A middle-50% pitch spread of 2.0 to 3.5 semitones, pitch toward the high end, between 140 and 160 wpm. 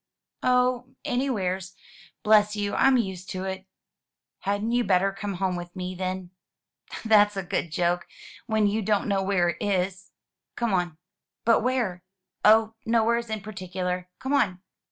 Yes: average, 3.2 semitones; high, 195 Hz; average, 150 wpm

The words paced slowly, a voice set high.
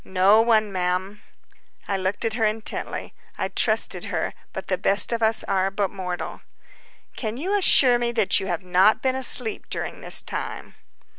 No: average, 170 wpm; high, 210 Hz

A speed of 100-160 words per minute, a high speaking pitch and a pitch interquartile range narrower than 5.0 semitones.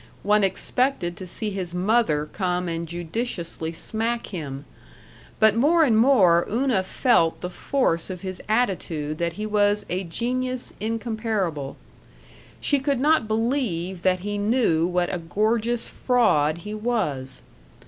No: average, 140 wpm; high, 205 Hz; wide, 5.4 semitones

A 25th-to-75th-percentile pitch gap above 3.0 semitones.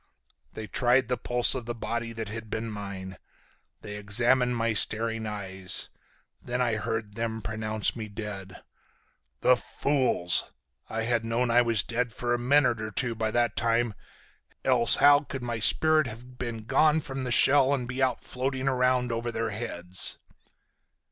No: narrow, 2.5 semitones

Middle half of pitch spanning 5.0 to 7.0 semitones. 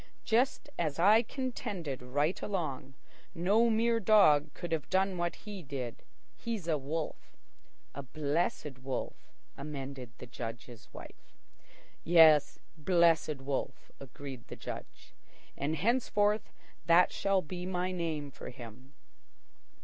Yes: wide, 5.5 semitones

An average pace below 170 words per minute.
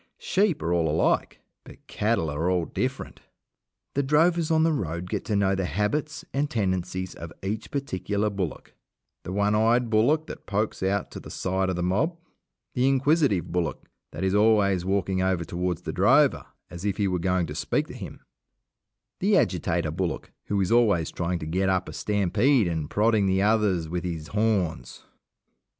No: average, 180 wpm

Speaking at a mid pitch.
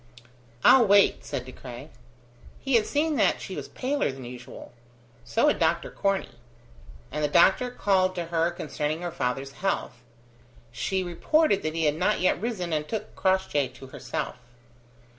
Yes: medium, 170 Hz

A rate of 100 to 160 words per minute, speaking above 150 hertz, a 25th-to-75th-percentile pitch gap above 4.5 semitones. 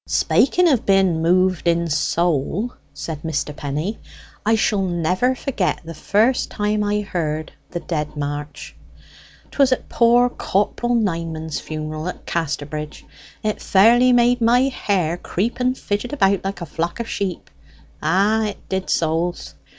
Yes: average, 145 wpm; medium, 185 Hz; wide, 5.6 semitones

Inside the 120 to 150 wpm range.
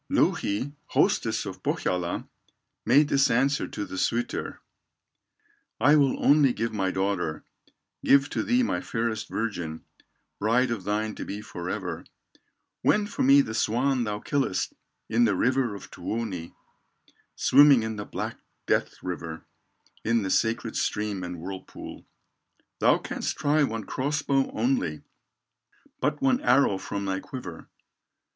Yes: average, 140 wpm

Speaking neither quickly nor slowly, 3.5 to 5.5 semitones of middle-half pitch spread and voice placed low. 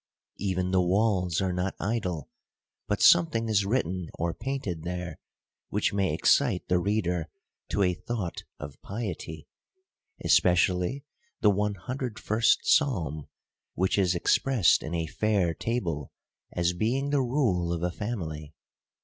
No: slow, 130 wpm; average, 4.3 semitones; very low, 95 Hz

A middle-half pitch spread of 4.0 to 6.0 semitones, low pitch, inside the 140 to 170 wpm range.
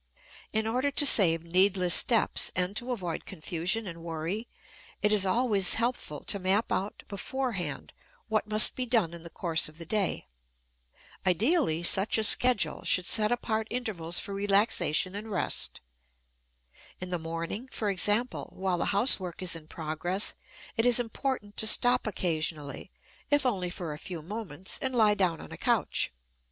No: average, 4.6 semitones; high, 195 Hz; average, 160 wpm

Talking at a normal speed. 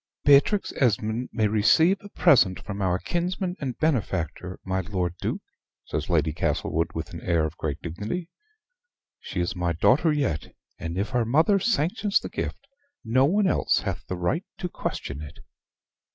Yes: average, 165 wpm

